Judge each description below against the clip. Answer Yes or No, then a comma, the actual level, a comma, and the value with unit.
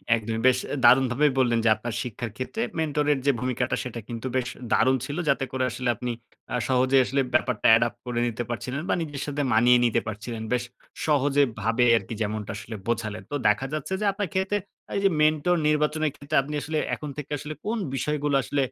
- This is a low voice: Yes, low, 130 Hz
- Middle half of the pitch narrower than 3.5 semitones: No, average, 3.9 semitones